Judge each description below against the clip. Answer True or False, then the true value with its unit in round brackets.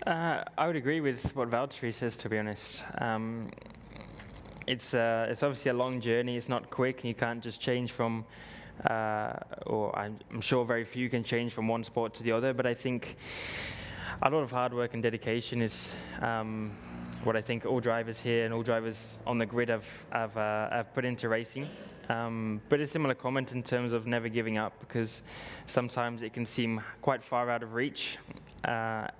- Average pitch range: False (1.8 semitones)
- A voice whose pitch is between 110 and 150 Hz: True (115 Hz)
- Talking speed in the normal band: True (195 wpm)